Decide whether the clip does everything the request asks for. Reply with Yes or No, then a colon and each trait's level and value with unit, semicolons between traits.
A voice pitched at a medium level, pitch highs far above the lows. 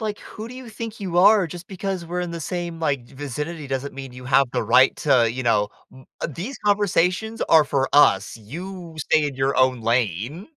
Yes: medium, 155 Hz; wide, 6.1 semitones